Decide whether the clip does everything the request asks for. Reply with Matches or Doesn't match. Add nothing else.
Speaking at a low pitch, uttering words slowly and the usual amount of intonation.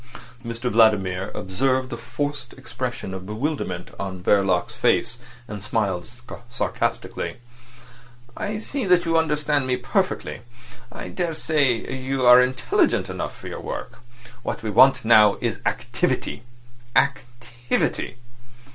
Matches